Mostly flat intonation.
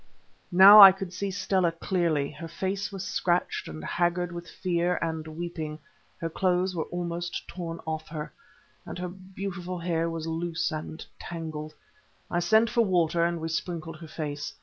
Yes: narrow, 2.1 semitones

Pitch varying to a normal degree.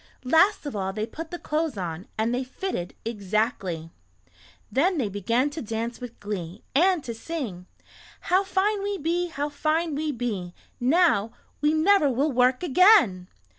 No: wide, 7.5 semitones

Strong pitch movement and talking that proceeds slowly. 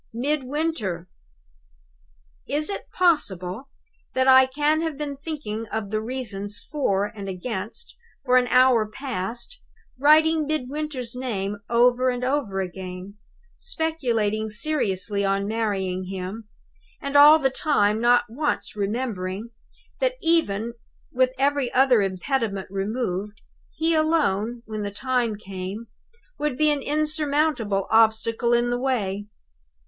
Yes: wide, 5.9 semitones; slow, 120 wpm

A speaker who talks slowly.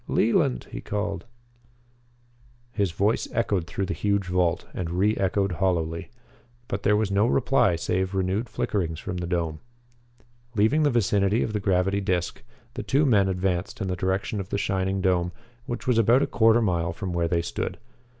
No: average, 175 wpm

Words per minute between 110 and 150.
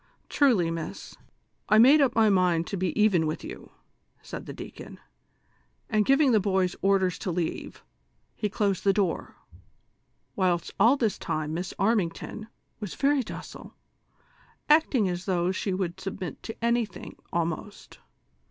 Yes: average, 145 wpm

